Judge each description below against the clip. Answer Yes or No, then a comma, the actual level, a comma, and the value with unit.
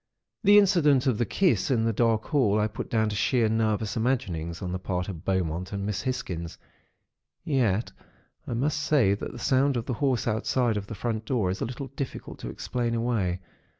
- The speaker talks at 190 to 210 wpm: Yes, average, 200 wpm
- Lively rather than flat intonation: No, average, 4.6 semitones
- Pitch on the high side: No, low, 115 Hz